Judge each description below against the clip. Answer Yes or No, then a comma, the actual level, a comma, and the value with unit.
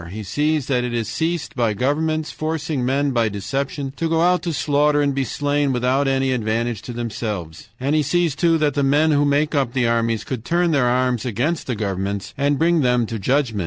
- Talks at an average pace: No, fast, 215 wpm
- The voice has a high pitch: No, low, 135 Hz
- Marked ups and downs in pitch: No, average, 4.1 semitones